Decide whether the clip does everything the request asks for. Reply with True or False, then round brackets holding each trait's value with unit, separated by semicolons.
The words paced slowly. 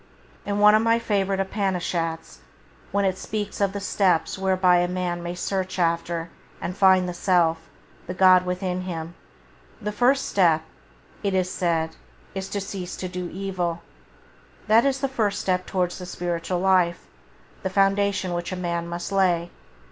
False (165 wpm)